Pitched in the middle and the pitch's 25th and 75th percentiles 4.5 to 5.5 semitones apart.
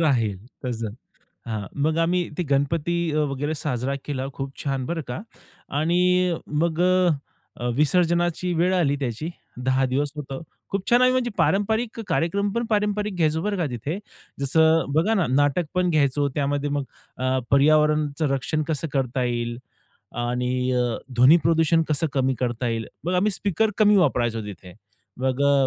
Yes: medium, 150 Hz; average, 5.2 semitones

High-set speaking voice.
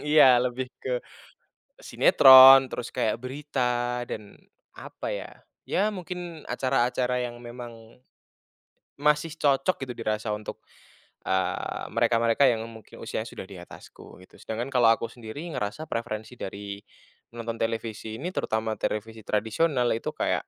No: low, 120 Hz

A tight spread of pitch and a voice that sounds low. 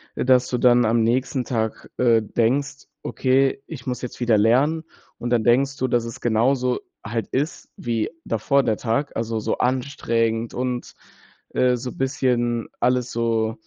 Yes: narrow, 2.1 semitones; low, 120 Hz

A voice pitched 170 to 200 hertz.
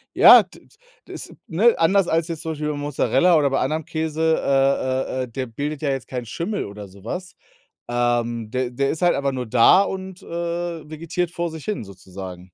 No: medium, 140 Hz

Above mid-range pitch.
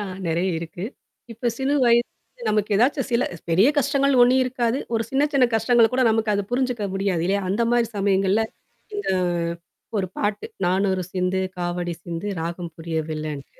Yes: high, 205 Hz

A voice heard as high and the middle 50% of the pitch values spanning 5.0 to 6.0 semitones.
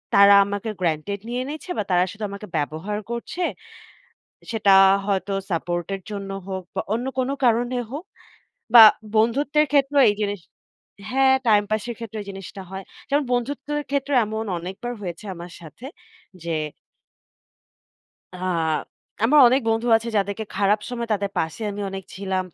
No: high, 210 Hz; average, 4.1 semitones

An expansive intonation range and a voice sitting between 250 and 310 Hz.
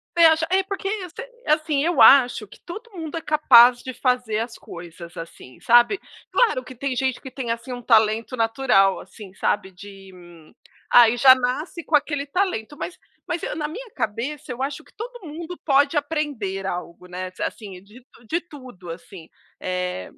Yes: wide, 6.6 semitones; very high, 255 Hz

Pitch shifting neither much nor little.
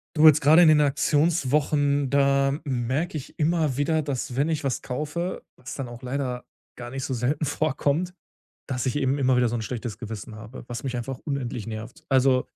Yes: average, 3.1 semitones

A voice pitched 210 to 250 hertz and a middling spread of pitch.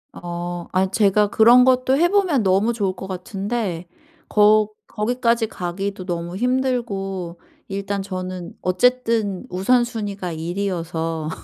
No: high, 200 Hz; average, 4.3 semitones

